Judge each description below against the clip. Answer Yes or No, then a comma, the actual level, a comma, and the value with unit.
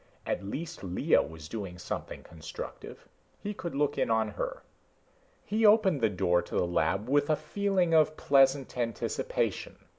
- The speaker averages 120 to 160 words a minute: Yes, average, 155 wpm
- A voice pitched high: No, low, 135 Hz